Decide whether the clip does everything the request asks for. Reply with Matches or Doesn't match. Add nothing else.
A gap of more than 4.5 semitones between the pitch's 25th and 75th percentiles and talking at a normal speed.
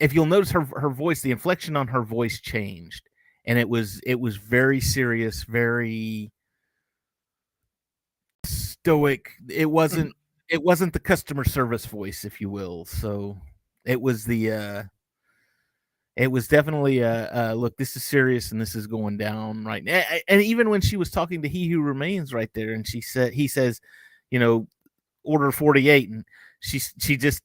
Matches